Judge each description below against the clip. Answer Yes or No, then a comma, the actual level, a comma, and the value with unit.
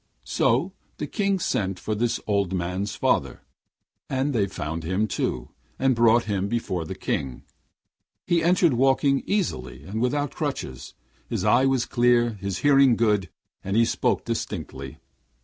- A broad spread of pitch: Yes, wide, 6.0 semitones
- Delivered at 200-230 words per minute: No, average, 150 wpm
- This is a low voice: Yes, low, 115 Hz